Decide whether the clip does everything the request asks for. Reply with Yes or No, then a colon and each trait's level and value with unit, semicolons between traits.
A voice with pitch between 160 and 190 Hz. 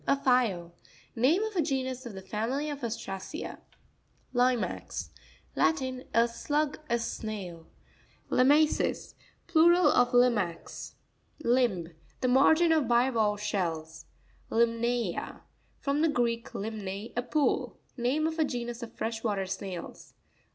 No: high, 240 Hz